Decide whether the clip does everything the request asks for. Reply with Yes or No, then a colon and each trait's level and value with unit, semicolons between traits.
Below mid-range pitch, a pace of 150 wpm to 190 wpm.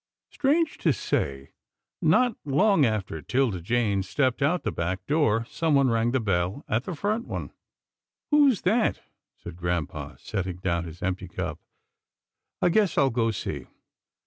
Yes: low, 120 Hz; average, 160 wpm